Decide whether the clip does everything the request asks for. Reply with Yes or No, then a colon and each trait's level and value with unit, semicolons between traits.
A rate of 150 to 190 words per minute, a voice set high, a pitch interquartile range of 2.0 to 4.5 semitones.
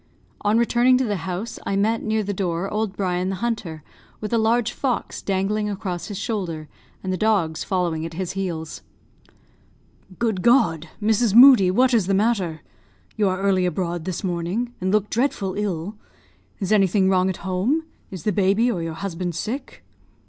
Yes: average, 175 wpm; high, 195 Hz; average, 3.4 semitones